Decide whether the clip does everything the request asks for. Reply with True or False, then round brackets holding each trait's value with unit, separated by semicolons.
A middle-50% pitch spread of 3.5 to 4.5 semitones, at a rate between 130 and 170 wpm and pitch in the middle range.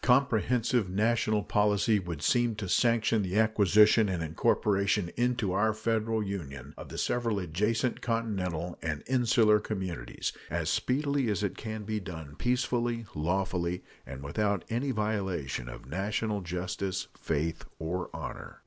False (4.2 semitones; 135 wpm; 105 Hz)